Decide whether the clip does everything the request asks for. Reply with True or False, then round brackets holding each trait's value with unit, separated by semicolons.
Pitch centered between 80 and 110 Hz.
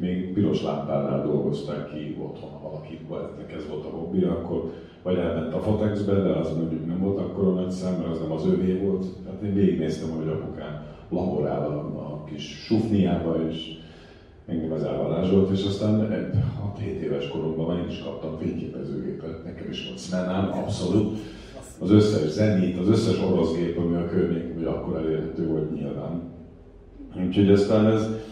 True (85 Hz)